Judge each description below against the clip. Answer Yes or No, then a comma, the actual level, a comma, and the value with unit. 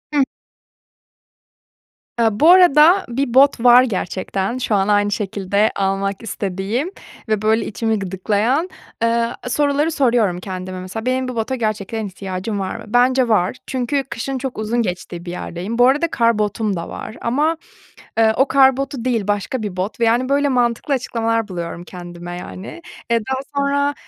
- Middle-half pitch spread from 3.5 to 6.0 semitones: Yes, average, 4.8 semitones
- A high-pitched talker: Yes, high, 225 Hz